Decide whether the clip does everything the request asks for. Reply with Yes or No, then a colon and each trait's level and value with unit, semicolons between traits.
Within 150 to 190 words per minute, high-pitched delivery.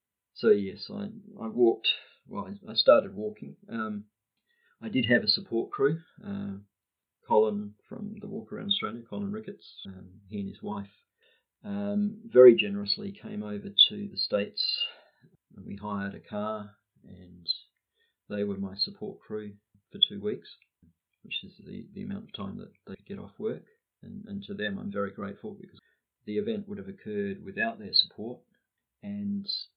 Yes: average, 165 wpm; high, 200 Hz